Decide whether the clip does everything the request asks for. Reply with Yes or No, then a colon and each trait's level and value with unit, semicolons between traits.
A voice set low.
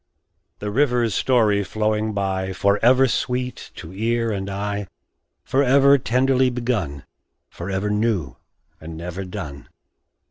Yes: low, 105 Hz